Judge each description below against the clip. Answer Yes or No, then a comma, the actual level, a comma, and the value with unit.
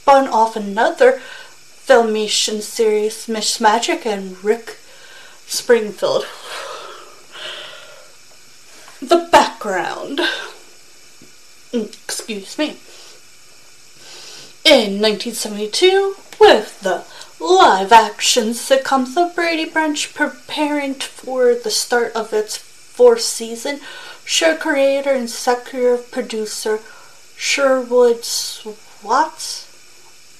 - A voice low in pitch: No, very high, 275 Hz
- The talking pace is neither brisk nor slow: No, slow, 75 wpm